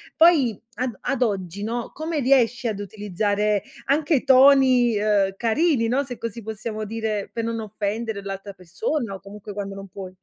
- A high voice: Yes, high, 225 Hz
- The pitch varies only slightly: No, average, 3.8 semitones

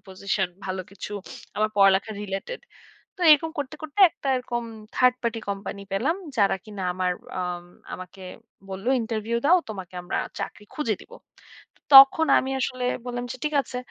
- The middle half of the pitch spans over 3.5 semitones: Yes, wide, 5.4 semitones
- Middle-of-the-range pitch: No, high, 220 Hz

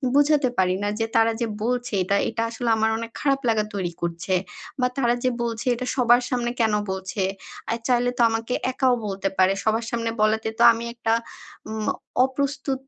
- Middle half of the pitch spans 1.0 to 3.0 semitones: Yes, narrow, 2.6 semitones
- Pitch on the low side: No, high, 230 Hz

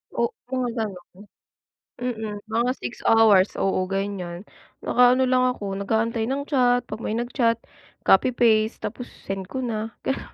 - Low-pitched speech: No, high, 225 Hz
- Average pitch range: Yes, average, 3.7 semitones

